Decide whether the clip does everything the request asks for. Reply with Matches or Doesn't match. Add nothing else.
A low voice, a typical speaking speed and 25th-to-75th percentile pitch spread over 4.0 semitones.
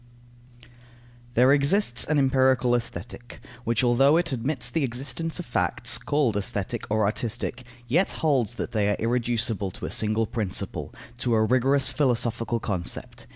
Doesn't match